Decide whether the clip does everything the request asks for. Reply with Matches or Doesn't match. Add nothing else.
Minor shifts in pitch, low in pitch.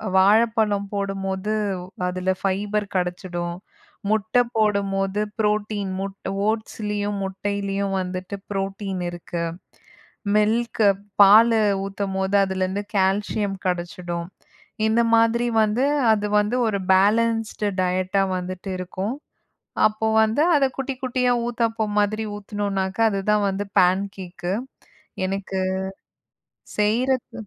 Doesn't match